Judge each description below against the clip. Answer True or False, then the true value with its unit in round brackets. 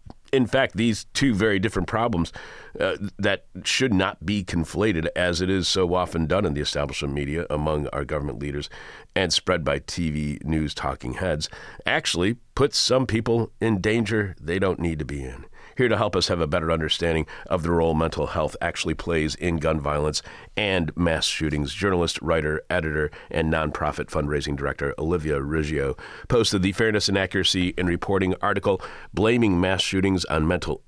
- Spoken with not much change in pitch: False (4.2 semitones)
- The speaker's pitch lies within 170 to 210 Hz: False (85 Hz)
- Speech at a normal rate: True (175 wpm)